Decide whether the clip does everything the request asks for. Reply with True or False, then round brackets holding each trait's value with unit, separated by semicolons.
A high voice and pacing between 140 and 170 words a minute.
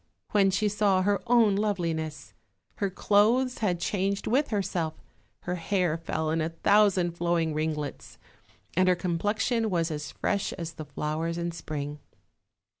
False (180 Hz; 150 wpm)